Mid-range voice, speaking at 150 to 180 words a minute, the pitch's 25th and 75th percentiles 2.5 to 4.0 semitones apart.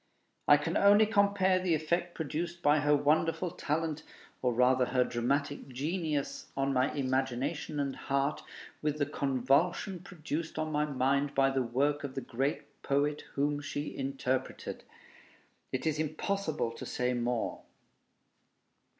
No: medium, 145 Hz; average, 140 wpm; average, 3.1 semitones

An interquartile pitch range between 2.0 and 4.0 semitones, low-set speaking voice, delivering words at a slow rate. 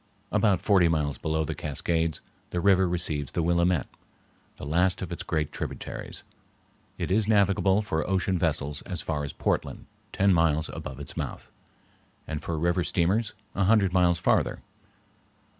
No: average, 3.2 semitones; very low, 85 Hz; average, 155 wpm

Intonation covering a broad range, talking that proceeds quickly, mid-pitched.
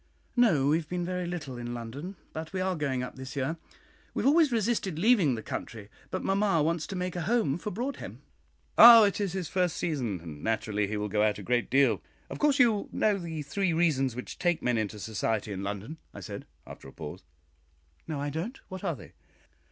Yes: wide, 7.8 semitones; fast, 215 wpm; medium, 160 Hz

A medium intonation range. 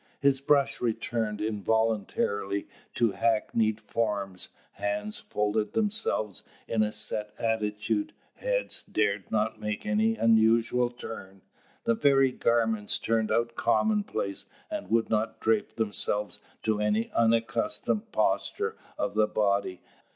No: narrow, 1.9 semitones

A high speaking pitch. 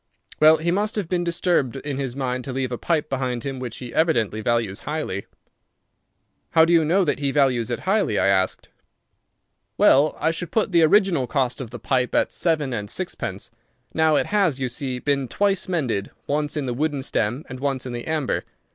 No: medium, 140 Hz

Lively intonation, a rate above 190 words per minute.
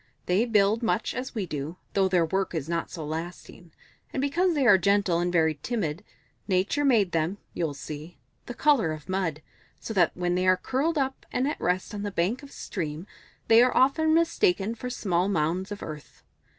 Yes: wide, 6.0 semitones; average, 200 wpm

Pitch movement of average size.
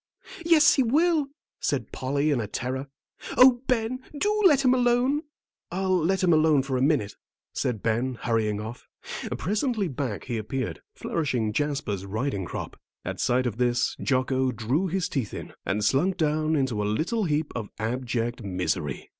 No: wide, 8.7 semitones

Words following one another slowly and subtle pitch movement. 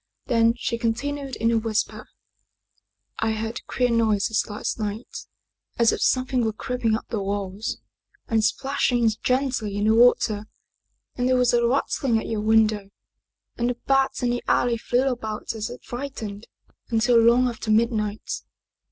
No: average, 160 wpm; narrow, 2.3 semitones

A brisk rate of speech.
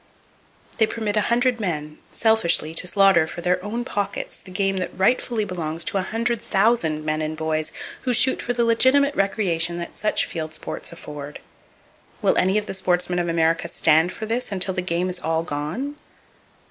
No: average, 185 wpm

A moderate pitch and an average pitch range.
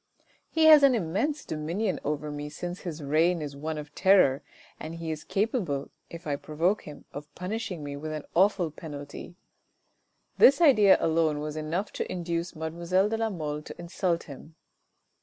Yes: medium, 165 Hz; average, 4.1 semitones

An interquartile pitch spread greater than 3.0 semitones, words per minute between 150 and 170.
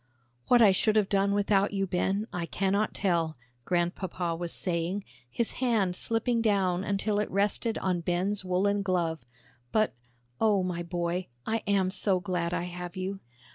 No: narrow, 2.5 semitones; average, 160 wpm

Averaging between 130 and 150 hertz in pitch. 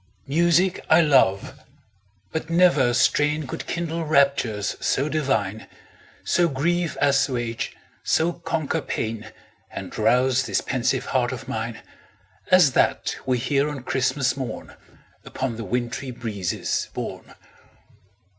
Yes: low, 135 Hz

